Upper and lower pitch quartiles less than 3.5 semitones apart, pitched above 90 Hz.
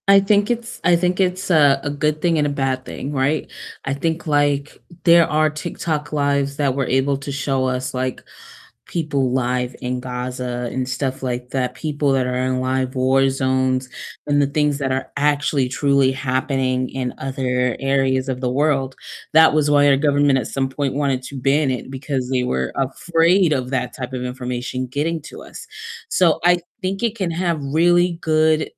Yes: average, 2.9 semitones; low, 135 Hz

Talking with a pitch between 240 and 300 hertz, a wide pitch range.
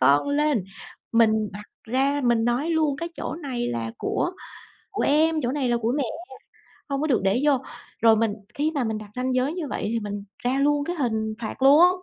No: very high, 255 Hz; average, 4.9 semitones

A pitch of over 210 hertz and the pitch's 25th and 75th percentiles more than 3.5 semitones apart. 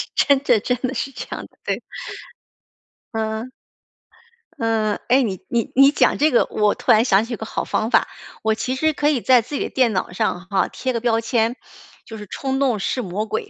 No: high, 230 Hz; average, 3.0 semitones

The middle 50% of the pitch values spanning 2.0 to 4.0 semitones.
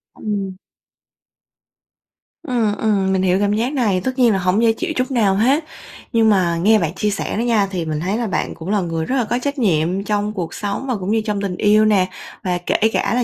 Yes: average, 3.4 semitones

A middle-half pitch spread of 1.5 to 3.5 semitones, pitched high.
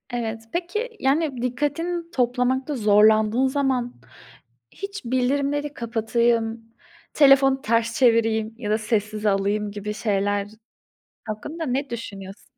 No: average, 4.2 semitones; high, 240 Hz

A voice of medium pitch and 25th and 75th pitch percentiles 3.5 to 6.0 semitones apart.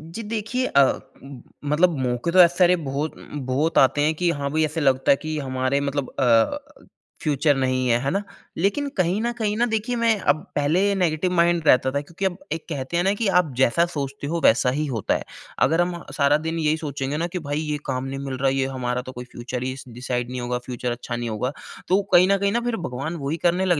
Yes: medium, 150 Hz; average, 5.1 semitones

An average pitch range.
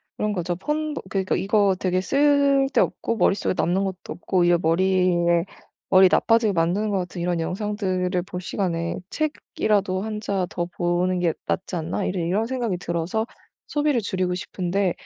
Yes: average, 3.3 semitones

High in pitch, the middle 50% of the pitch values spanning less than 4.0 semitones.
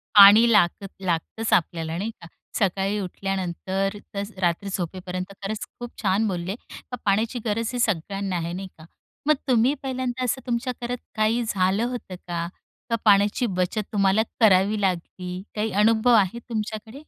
Yes: high, 200 Hz; average, 3.5 semitones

